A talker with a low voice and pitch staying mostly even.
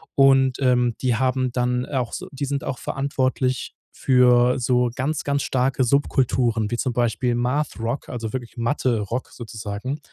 Yes: low, 125 Hz; narrow, 1.8 semitones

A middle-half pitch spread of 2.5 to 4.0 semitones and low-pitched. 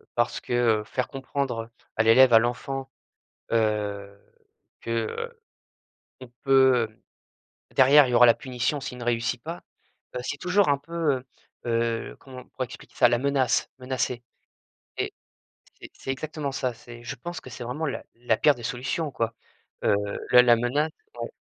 Yes: average, 2.8 semitones; low, 125 Hz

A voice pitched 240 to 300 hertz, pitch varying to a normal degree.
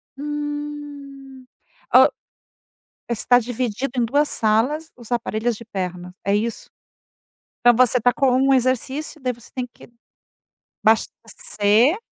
Yes: very high, 250 Hz; average, 3.8 semitones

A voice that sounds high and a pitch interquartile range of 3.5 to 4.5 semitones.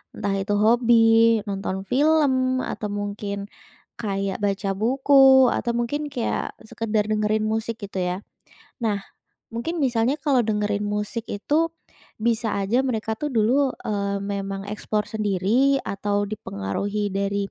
No: high, 215 Hz; average, 3.1 semitones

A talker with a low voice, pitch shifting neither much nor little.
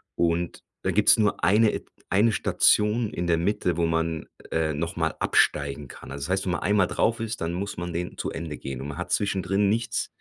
Yes: very low, 85 Hz; average, 4.0 semitones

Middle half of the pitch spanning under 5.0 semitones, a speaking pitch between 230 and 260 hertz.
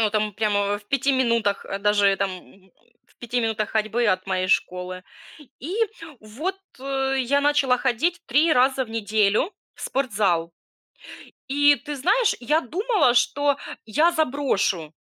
No: wide, 5.6 semitones; high, 240 Hz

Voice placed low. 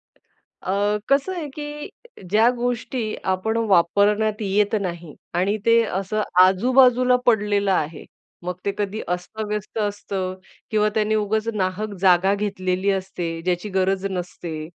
No: high, 205 Hz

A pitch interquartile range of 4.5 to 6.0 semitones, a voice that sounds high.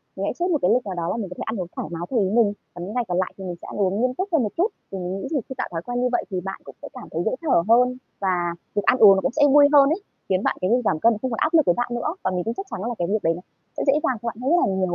Yes: average, 5.3 semitones; high, 225 Hz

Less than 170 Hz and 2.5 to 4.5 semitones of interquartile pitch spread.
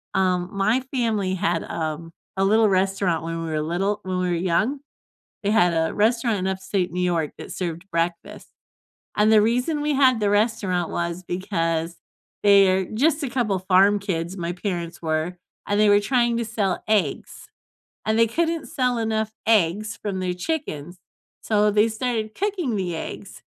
No: high, 195 Hz; average, 4.0 semitones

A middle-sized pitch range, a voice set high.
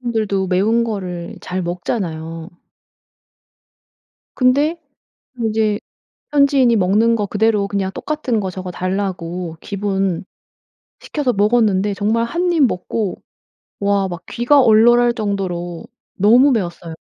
Yes: average, 4.1 semitones; high, 205 Hz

